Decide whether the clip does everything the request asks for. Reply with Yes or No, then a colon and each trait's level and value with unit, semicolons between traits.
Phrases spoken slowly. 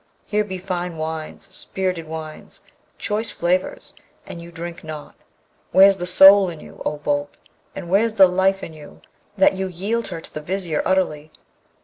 No: average, 165 wpm